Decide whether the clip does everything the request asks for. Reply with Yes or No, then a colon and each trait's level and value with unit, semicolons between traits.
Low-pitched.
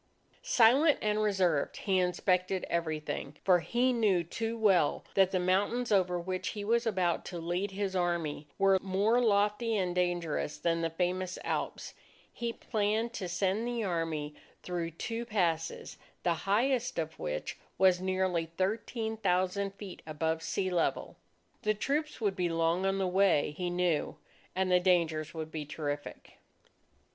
No: medium, 185 Hz